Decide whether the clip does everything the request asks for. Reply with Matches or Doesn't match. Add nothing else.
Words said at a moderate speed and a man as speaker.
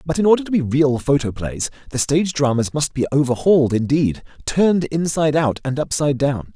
Matches